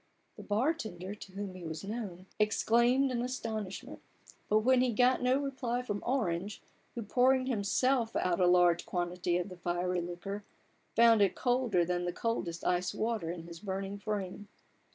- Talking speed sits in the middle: Yes, average, 170 wpm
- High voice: Yes, high, 205 Hz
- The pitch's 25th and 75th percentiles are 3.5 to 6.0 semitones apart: Yes, average, 5.1 semitones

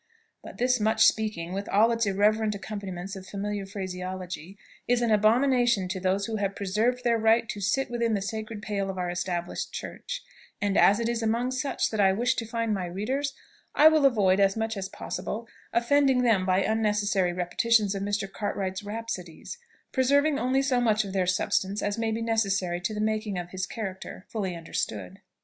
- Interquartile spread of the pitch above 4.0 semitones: No, average, 3.2 semitones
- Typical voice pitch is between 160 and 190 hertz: No, high, 210 Hz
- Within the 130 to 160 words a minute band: No, average, 185 wpm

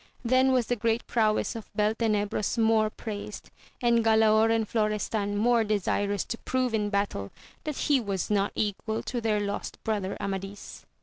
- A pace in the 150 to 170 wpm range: Yes, average, 160 wpm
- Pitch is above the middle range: Yes, high, 215 Hz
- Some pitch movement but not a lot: No, narrow, 2.0 semitones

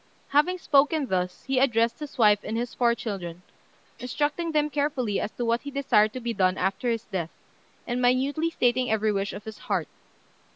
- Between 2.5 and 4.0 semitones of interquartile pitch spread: No, average, 5.1 semitones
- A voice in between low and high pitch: No, high, 240 Hz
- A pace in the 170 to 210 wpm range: Yes, average, 190 wpm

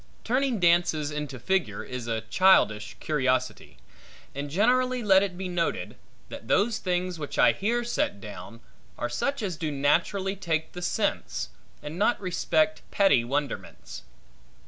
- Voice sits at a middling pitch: Yes, medium, 175 Hz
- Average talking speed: Yes, average, 145 wpm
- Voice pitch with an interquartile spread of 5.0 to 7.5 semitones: Yes, wide, 5.5 semitones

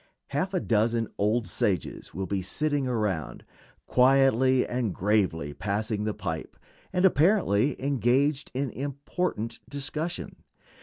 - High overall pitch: No, low, 120 Hz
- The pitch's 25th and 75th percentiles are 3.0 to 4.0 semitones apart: No, average, 5.3 semitones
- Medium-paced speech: No, slow, 115 wpm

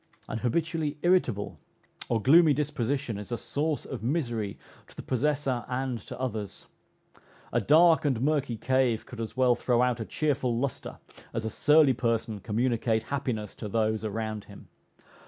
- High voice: No, low, 125 Hz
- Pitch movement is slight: No, average, 4.2 semitones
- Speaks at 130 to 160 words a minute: Yes, average, 155 wpm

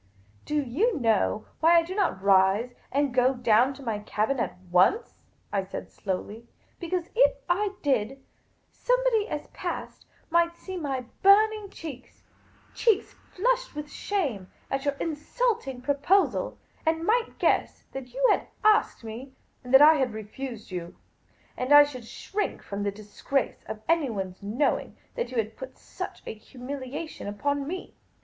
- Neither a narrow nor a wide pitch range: No, wide, 7.4 semitones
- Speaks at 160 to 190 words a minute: Yes, average, 165 wpm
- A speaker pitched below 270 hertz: No, very high, 275 Hz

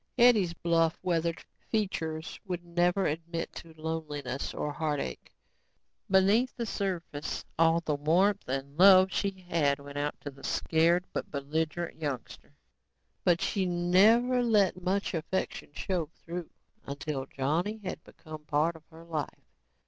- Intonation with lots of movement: No, average, 3.7 semitones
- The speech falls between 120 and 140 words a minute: Yes, slow, 135 wpm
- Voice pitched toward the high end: No, medium, 170 Hz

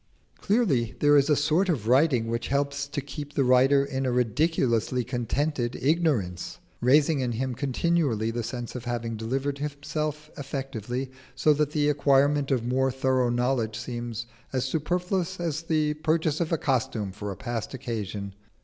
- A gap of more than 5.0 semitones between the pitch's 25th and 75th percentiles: No, average, 3.8 semitones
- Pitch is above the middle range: No, low, 135 Hz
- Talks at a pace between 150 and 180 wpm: Yes, average, 160 wpm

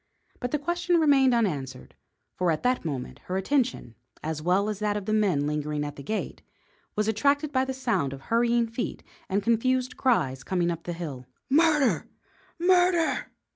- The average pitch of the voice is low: No, high, 215 Hz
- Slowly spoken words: No, average, 175 wpm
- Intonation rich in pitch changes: Yes, wide, 8.8 semitones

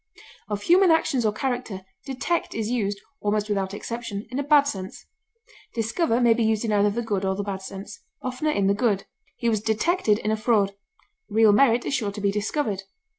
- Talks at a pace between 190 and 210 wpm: Yes, average, 200 wpm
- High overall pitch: Yes, high, 220 Hz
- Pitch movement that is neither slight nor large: Yes, average, 3.4 semitones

